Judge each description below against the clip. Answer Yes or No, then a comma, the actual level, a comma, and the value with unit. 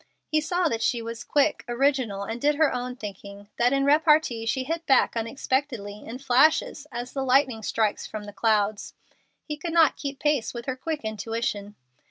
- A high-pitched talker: Yes, very high, 250 Hz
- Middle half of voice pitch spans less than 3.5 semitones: No, average, 4.5 semitones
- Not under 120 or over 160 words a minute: No, average, 185 wpm